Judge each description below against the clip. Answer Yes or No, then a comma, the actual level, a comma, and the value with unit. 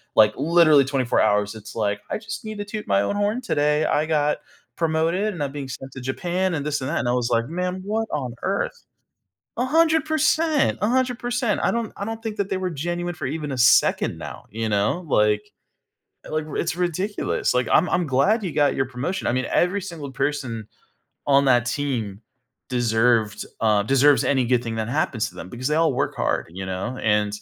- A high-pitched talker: No, medium, 145 Hz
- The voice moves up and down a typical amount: No, wide, 7.4 semitones